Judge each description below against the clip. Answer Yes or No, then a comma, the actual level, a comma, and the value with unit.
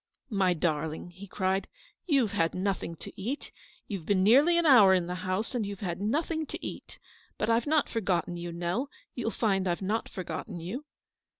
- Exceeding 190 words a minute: Yes, average, 200 wpm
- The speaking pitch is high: Yes, high, 195 Hz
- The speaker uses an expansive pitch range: No, average, 4.9 semitones